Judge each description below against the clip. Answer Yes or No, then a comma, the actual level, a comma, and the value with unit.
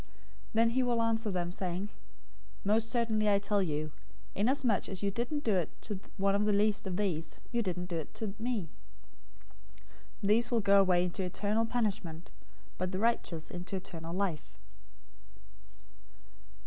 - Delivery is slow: No, average, 160 wpm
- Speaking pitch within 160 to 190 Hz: No, high, 200 Hz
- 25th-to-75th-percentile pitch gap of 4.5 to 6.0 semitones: No, average, 3.8 semitones